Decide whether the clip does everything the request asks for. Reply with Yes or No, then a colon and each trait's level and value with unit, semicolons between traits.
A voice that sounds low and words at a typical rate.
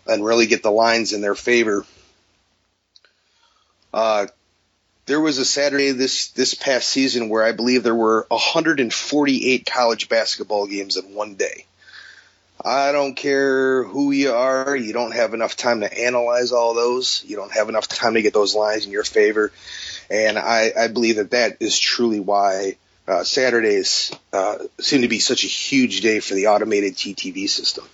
Yes: low, 120 Hz; average, 170 wpm